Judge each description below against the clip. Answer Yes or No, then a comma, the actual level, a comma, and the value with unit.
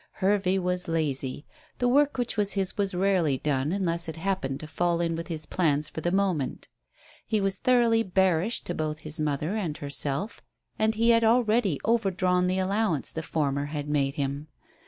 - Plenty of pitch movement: No, average, 4.9 semitones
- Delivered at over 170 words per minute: Yes, average, 180 wpm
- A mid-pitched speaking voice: Yes, medium, 180 Hz